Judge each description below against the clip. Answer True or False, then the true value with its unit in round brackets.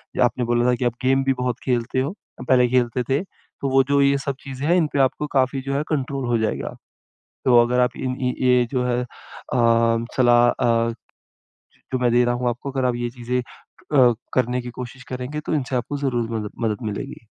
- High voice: False (125 Hz)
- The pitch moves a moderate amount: False (1.8 semitones)